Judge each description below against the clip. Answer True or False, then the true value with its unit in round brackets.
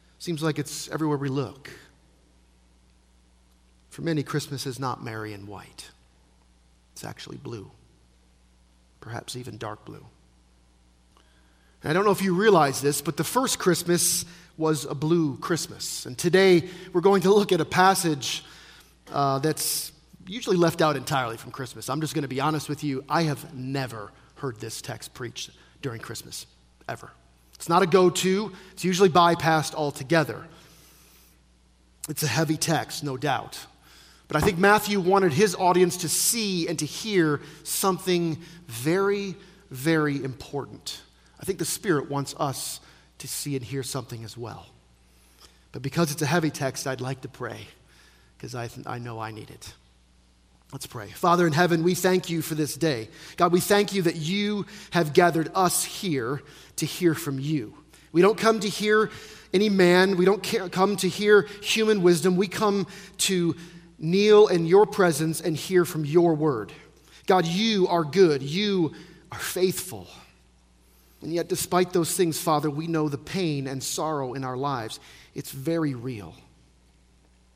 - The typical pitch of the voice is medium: True (155 Hz)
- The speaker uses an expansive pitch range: True (7.8 semitones)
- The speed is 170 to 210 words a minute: False (160 wpm)